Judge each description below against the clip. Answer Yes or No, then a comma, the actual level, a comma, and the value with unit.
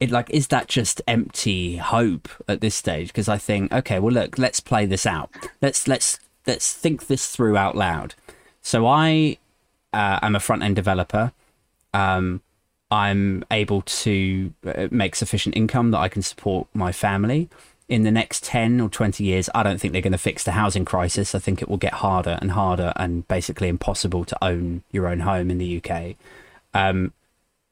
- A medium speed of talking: Yes, average, 180 wpm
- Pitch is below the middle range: Yes, low, 100 Hz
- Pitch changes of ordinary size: Yes, average, 3.4 semitones